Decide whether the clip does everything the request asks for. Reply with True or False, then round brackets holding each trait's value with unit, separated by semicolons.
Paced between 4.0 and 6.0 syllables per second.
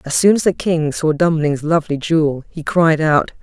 True (5.0 syllables/s)